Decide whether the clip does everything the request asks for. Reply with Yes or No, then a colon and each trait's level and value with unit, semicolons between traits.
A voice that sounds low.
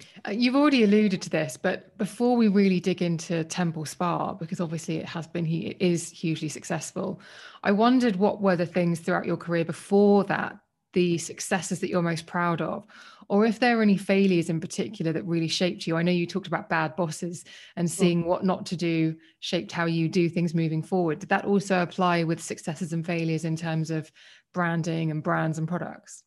No: medium, 175 Hz